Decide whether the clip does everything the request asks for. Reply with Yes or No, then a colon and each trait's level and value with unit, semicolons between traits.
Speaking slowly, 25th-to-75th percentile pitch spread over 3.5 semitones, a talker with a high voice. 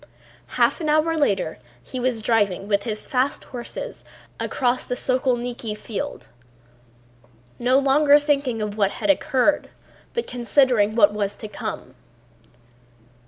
Yes: slow, 125 wpm; average, 4.7 semitones; high, 245 Hz